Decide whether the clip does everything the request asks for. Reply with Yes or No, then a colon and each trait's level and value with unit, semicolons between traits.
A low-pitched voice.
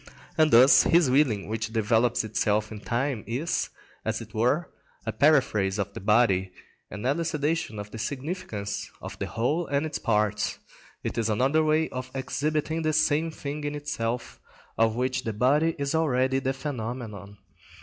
Yes: low, 130 Hz